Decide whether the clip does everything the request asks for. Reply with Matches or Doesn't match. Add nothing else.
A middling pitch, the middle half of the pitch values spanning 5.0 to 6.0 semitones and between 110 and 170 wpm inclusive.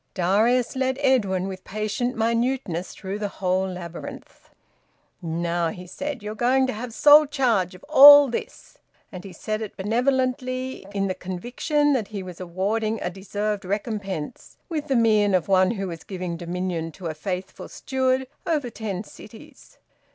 Doesn't match